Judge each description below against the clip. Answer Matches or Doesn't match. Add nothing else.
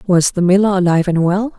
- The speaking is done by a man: Doesn't match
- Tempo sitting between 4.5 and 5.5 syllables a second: Doesn't match